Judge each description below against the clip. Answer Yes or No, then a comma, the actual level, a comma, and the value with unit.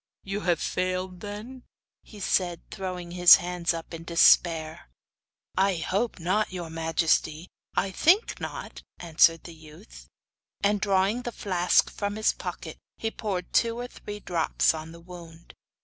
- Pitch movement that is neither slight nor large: Yes, average, 3.4 semitones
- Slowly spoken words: No, average, 150 wpm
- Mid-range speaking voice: Yes, medium, 180 Hz